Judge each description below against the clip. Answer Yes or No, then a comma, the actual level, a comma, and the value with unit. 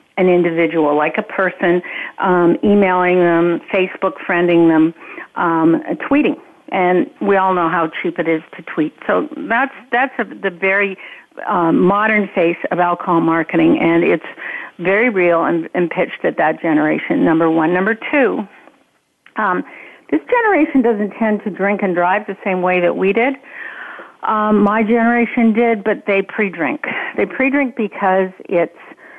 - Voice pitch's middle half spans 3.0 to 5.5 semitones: Yes, average, 4.3 semitones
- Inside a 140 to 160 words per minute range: Yes, average, 155 wpm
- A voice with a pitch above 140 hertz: Yes, high, 190 Hz